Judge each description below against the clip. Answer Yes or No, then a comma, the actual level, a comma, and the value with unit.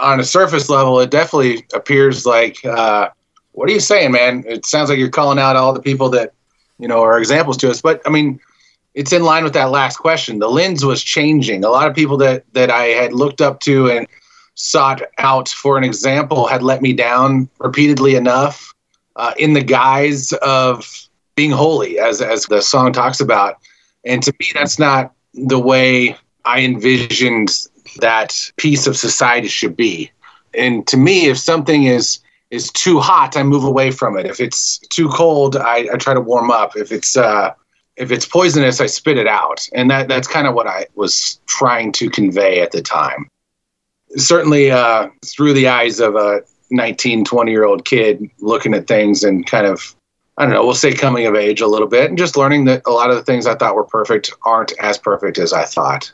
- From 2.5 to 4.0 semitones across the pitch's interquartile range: Yes, average, 3.0 semitones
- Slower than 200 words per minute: No, fast, 205 wpm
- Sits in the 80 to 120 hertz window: No, low, 130 Hz